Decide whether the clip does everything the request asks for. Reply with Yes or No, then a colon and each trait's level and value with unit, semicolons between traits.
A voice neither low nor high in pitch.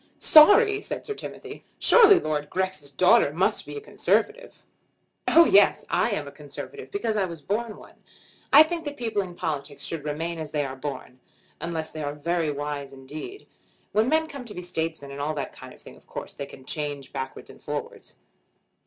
Yes: medium, 165 Hz